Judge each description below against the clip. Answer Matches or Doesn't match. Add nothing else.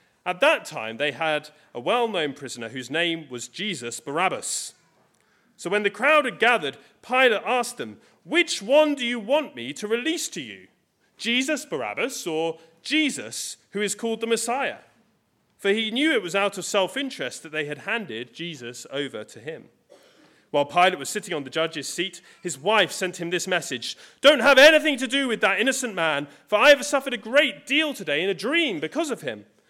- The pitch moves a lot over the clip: Matches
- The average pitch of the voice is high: Matches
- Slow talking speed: Doesn't match